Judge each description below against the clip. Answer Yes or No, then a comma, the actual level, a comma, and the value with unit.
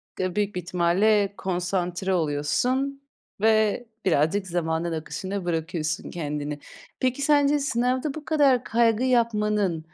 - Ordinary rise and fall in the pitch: No, wide, 6.2 semitones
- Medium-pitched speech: No, high, 195 Hz